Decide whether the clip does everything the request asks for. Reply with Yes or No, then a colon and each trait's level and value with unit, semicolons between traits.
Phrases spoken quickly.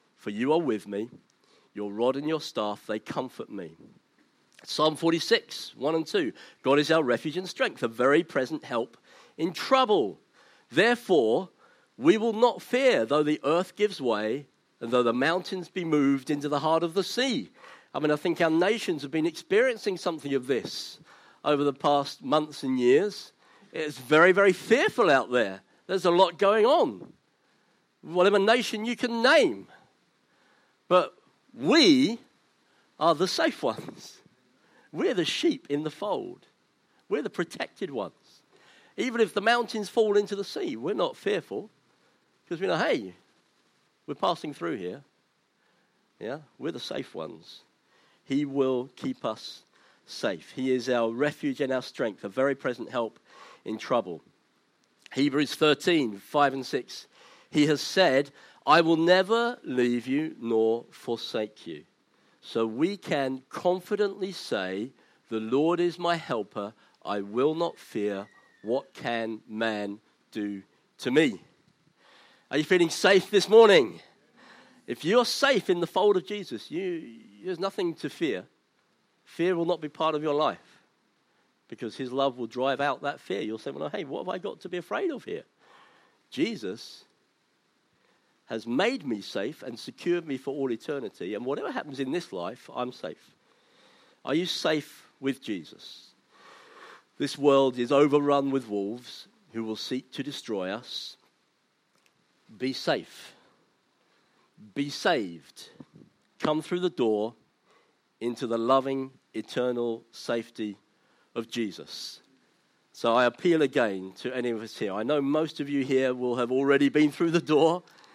No: average, 155 wpm